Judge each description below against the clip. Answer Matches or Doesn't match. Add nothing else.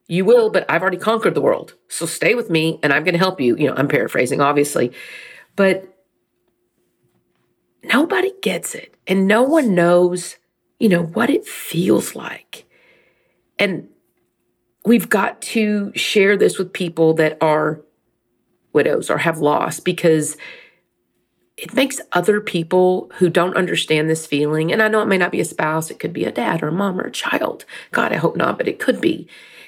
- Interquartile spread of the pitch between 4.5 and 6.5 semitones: Matches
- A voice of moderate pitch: Matches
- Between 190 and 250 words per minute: Doesn't match